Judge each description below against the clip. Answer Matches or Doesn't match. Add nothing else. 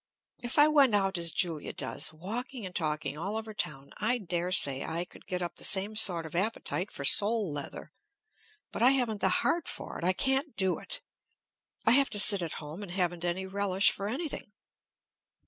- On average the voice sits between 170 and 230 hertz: Matches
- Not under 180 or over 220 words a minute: Matches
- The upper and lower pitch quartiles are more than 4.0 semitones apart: Matches